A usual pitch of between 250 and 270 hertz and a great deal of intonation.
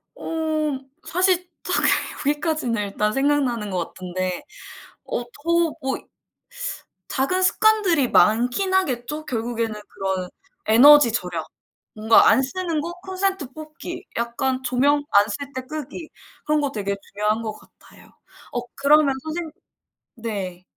Yes: very high, 265 Hz; wide, 5.9 semitones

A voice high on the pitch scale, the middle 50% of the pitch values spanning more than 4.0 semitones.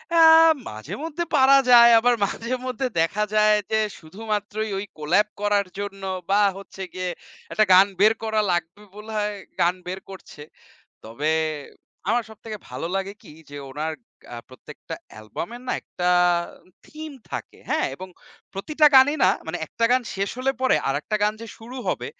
Yes: high, 210 Hz; average, 4.5 semitones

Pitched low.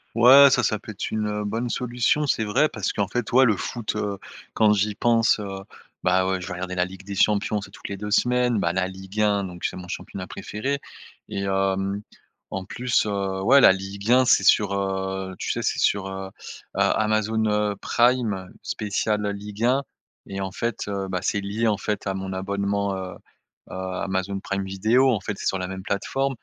Yes: low, 100 Hz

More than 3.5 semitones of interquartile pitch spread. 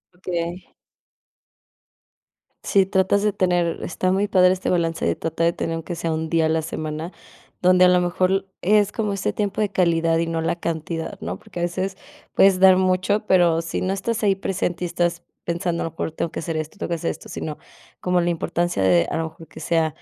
No: narrow, 2.4 semitones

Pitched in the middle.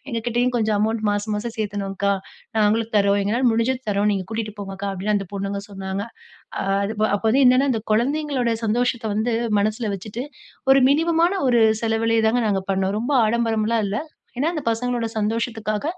No: high, 220 Hz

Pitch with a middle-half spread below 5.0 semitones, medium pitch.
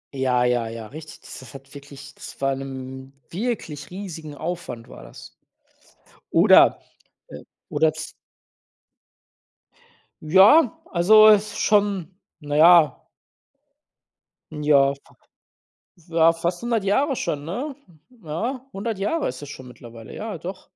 No: wide, 6.6 semitones; medium, 160 Hz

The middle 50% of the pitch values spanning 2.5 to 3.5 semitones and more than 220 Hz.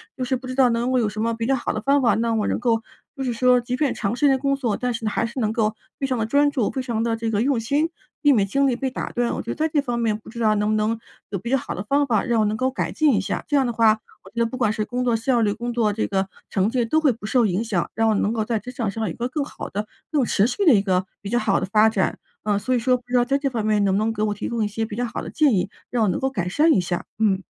Yes: average, 3.2 semitones; high, 230 Hz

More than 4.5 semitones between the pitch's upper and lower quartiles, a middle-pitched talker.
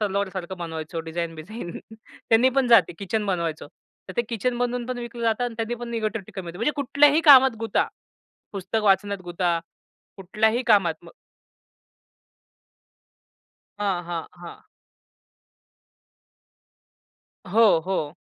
No: average, 5.1 semitones; high, 205 Hz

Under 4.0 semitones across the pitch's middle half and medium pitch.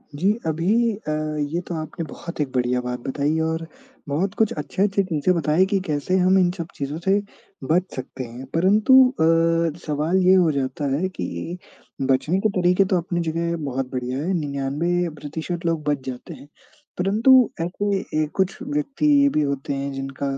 No: average, 4.8 semitones; medium, 165 Hz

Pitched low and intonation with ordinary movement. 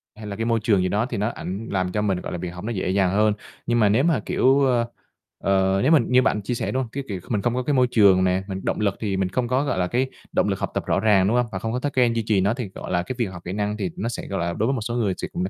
Yes: low, 105 Hz; average, 4.1 semitones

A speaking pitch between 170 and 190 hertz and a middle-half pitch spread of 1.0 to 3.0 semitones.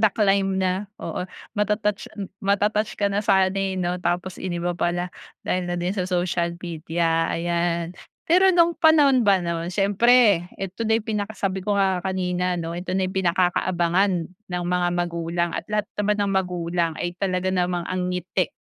Yes: medium, 185 Hz; narrow, 2.4 semitones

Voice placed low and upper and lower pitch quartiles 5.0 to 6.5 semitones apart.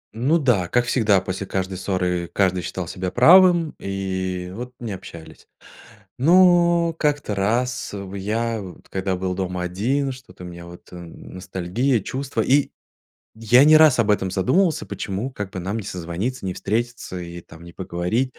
Yes: low, 100 Hz; wide, 5.6 semitones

